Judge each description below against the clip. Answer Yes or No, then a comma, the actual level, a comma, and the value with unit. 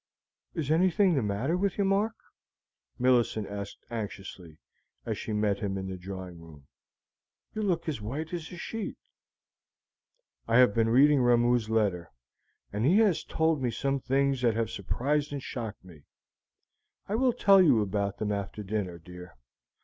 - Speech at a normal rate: Yes, average, 160 wpm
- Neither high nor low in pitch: No, low, 120 Hz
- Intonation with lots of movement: Yes, wide, 7.7 semitones